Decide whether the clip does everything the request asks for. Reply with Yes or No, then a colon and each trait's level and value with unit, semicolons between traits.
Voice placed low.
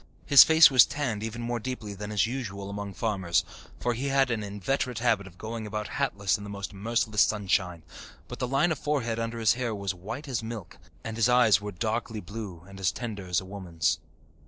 Yes: low, 110 Hz